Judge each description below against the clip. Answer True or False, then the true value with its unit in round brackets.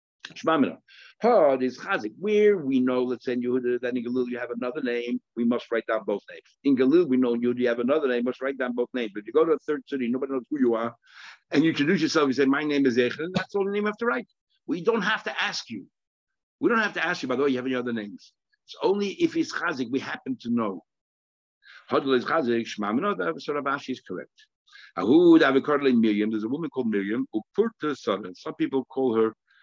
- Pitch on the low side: True (130 Hz)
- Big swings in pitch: True (8.4 semitones)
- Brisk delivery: True (250 wpm)